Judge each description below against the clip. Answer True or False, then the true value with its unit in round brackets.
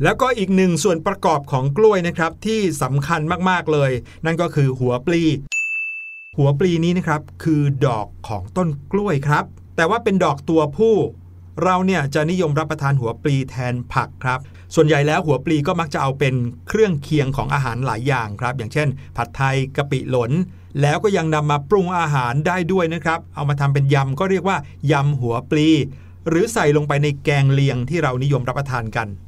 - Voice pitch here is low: False (145 Hz)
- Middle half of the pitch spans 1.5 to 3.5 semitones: False (4.6 semitones)